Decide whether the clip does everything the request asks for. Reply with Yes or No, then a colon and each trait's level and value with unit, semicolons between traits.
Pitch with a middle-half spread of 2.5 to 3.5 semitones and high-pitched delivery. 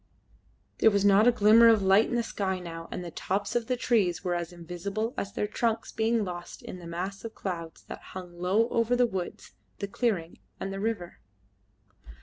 No: average, 4.1 semitones; high, 200 Hz